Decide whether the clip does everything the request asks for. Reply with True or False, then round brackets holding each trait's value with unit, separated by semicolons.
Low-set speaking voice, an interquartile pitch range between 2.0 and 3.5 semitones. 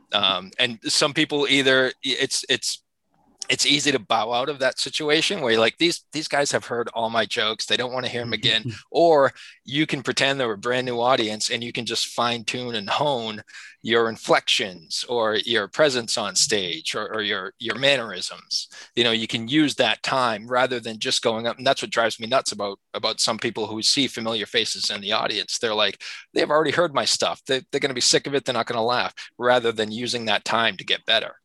True (125 Hz; 3.2 semitones)